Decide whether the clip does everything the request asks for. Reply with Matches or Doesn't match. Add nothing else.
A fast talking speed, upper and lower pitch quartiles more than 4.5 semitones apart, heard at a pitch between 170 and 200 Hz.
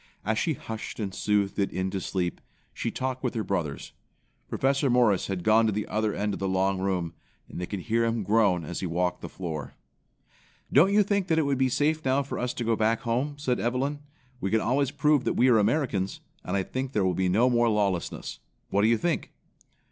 Doesn't match